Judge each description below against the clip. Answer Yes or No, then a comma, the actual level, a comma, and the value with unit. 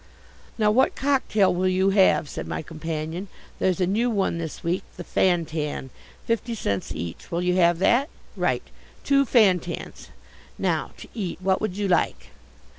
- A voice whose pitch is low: No, medium, 185 Hz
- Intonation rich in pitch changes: No, average, 4.0 semitones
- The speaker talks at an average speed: Yes, average, 160 wpm